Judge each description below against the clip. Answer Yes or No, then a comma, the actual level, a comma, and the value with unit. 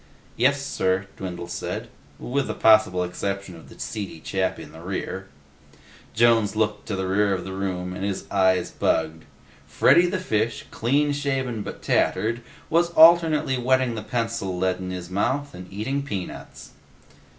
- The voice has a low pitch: Yes, low, 105 Hz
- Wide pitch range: Yes, wide, 5.8 semitones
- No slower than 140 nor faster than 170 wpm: Yes, average, 160 wpm